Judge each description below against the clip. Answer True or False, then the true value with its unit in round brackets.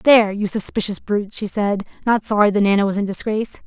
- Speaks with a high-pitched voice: True (205 Hz)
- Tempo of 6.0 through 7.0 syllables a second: True (6.3 syllables/s)